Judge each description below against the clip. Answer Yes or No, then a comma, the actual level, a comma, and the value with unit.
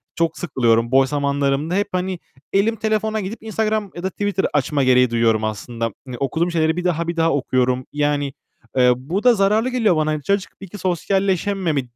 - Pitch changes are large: Yes, wide, 6.6 semitones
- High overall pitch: No, medium, 165 Hz